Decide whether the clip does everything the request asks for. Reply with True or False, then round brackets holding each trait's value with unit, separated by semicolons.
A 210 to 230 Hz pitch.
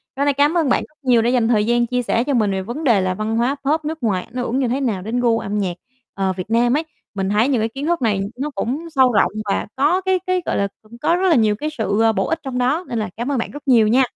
False (245 Hz)